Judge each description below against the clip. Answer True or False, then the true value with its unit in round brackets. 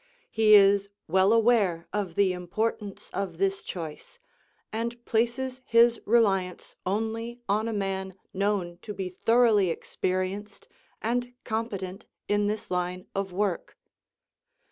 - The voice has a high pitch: True (205 Hz)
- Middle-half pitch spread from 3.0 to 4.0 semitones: True (3.3 semitones)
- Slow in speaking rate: True (120 wpm)